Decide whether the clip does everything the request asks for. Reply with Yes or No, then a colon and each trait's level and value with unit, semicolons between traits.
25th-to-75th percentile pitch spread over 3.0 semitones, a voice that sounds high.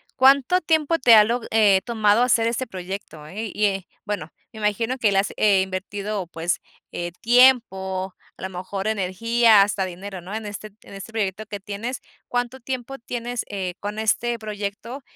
Yes: average, 3.6 semitones; high, 210 Hz